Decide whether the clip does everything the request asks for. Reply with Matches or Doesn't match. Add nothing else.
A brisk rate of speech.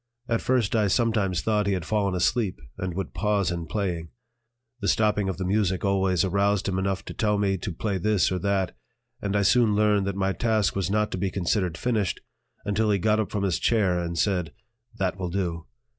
Matches